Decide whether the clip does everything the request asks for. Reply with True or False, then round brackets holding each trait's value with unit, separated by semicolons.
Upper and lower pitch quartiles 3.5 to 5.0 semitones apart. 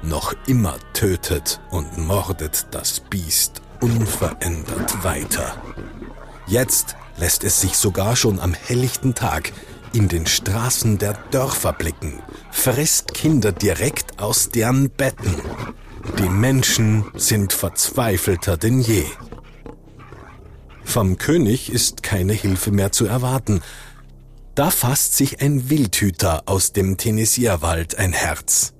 True (4.2 semitones)